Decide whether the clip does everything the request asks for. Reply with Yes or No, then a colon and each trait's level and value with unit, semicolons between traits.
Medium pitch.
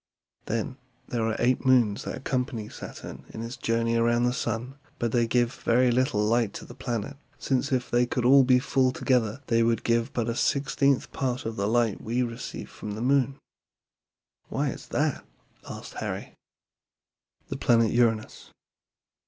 No: low, 120 Hz